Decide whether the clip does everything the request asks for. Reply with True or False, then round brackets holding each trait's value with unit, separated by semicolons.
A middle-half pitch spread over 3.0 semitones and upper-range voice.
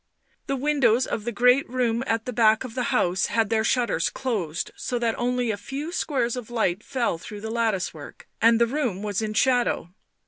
False (2.7 semitones; 235 Hz)